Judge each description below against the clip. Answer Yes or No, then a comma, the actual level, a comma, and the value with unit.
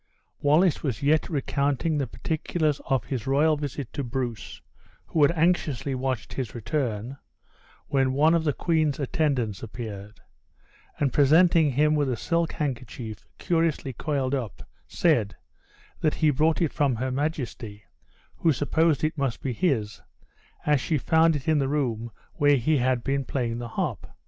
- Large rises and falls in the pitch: No, average, 3.8 semitones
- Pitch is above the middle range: No, medium, 140 Hz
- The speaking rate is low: No, average, 155 wpm